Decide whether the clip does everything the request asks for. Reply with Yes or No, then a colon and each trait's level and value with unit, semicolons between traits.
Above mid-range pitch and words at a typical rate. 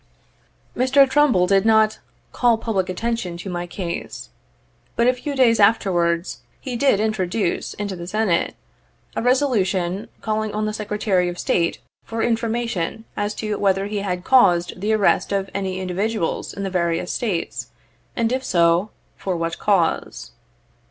Yes: high, 205 Hz; average, 160 wpm